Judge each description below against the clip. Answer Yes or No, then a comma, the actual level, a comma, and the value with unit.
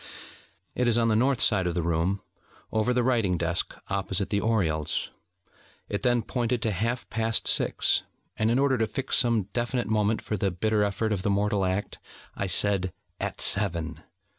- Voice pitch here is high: No, low, 105 Hz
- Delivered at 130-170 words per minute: No, average, 180 wpm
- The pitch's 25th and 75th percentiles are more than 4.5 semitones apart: No, average, 3.6 semitones